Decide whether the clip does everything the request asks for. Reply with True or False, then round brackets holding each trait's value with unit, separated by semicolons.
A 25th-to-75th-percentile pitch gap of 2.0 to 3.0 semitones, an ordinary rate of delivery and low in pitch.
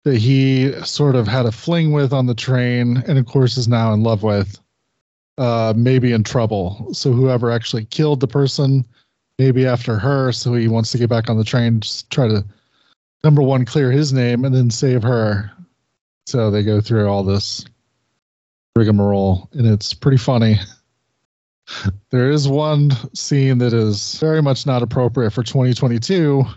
False (3.4 semitones; 170 wpm; 125 Hz)